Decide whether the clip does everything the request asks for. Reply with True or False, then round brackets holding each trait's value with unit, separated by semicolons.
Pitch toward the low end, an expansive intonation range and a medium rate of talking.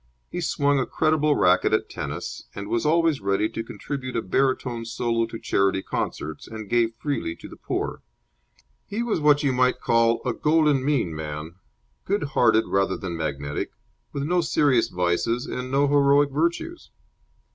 True (125 Hz; 6.5 semitones; 160 wpm)